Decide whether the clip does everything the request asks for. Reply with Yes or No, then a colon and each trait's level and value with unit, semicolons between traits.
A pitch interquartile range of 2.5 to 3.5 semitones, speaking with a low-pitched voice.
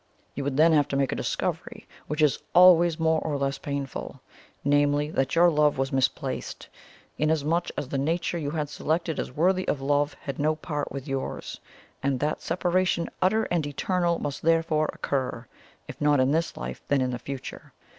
No: average, 3.0 semitones; medium, 150 Hz